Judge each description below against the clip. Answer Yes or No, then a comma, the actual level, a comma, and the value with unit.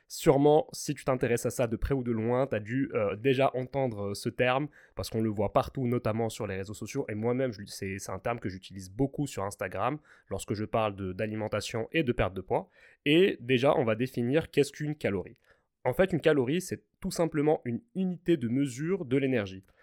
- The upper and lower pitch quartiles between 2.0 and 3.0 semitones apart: No, average, 4.7 semitones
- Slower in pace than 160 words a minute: No, average, 215 wpm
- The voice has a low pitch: Yes, low, 125 Hz